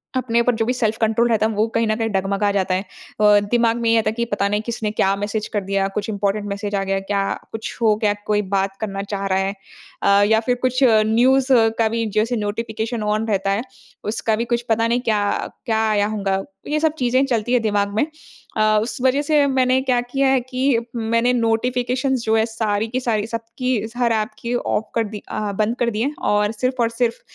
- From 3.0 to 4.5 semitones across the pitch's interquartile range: No, narrow, 2.6 semitones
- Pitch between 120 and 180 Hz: No, high, 225 Hz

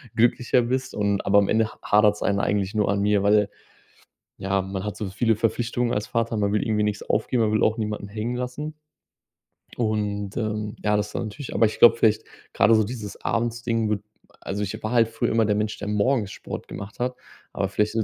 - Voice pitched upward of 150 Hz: No, low, 105 Hz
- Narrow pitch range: Yes, narrow, 2.0 semitones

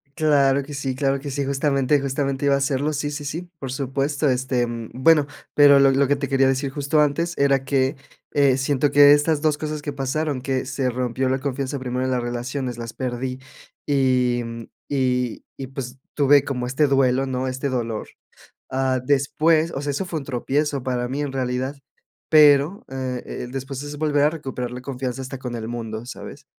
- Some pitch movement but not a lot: No, narrow, 2.1 semitones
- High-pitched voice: No, low, 135 Hz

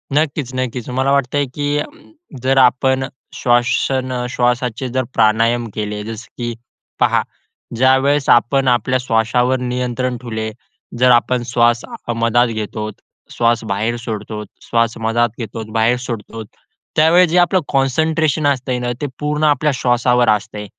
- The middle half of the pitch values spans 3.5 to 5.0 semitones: No, narrow, 2.5 semitones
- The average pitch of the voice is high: No, low, 125 Hz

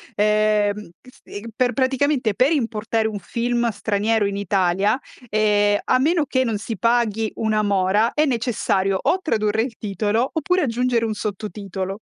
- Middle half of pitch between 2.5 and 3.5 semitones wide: Yes, average, 2.9 semitones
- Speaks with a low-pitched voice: No, high, 220 Hz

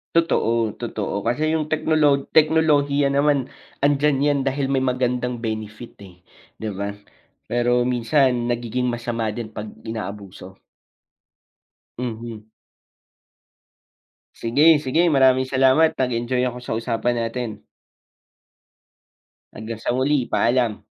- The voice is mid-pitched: No, low, 125 Hz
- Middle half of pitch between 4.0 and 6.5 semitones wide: No, average, 3.3 semitones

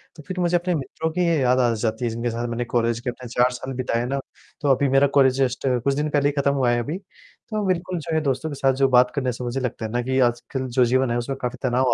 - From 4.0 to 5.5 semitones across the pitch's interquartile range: No, average, 2.9 semitones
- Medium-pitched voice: No, low, 130 Hz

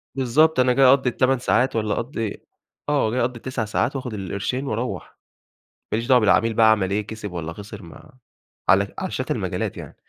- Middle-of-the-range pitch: No, low, 115 Hz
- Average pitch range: Yes, average, 3.5 semitones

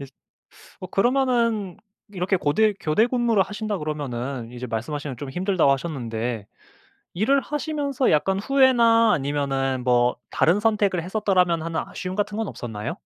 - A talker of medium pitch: Yes, medium, 180 Hz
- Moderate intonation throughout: No, wide, 8.2 semitones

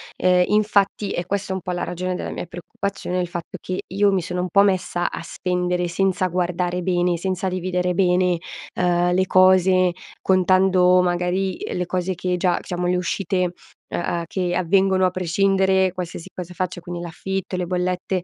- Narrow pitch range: Yes, narrow, 1.1 semitones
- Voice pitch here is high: No, medium, 180 Hz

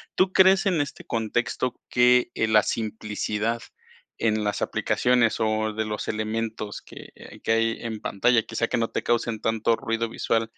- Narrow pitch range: Yes, narrow, 1.6 semitones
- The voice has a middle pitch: No, low, 115 Hz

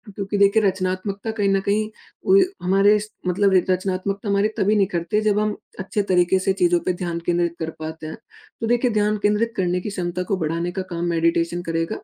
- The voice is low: No, high, 190 Hz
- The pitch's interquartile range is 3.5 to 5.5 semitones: No, average, 2.9 semitones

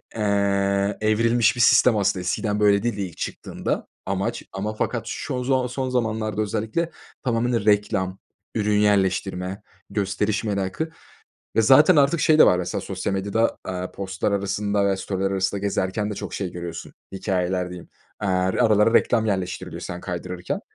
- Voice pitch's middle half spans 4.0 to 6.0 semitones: No, average, 2.8 semitones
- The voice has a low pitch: Yes, low, 100 Hz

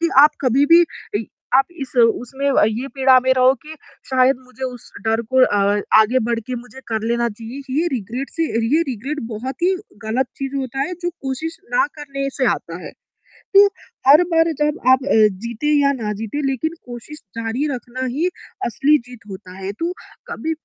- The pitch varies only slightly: No, average, 3.7 semitones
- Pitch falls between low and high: No, very high, 260 Hz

